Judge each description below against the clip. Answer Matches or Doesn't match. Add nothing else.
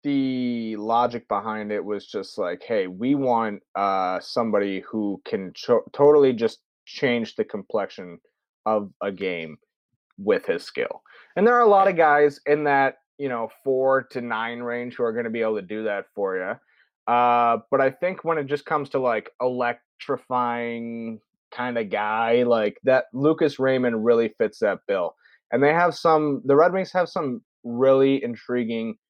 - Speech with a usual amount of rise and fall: Matches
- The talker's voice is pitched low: Matches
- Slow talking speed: Doesn't match